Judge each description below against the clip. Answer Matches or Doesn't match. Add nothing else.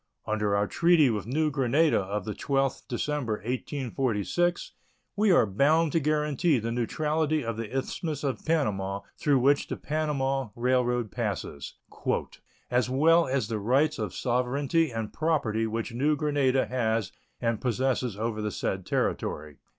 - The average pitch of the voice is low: Matches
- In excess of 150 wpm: Doesn't match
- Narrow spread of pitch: Doesn't match